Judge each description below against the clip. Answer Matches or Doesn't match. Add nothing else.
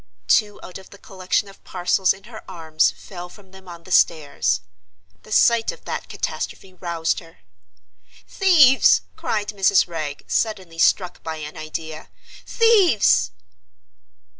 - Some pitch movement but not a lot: Matches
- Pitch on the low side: Doesn't match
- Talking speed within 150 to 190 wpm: Doesn't match